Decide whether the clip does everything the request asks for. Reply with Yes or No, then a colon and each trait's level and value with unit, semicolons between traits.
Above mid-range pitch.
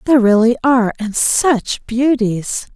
Yes: high, 235 Hz